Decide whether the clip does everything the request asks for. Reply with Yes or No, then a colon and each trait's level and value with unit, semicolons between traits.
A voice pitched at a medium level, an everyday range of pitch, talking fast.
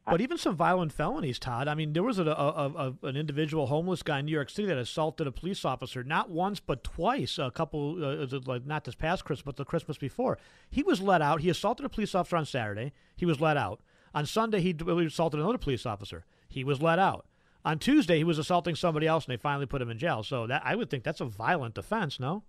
Yes: medium, 155 Hz; average, 4.0 semitones; fast, 250 wpm